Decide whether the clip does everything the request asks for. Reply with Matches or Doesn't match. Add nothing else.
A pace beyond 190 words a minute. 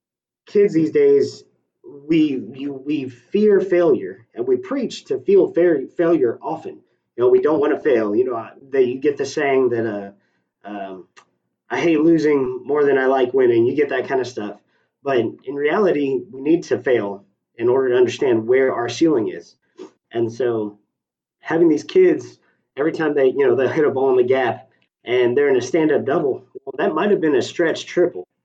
Matches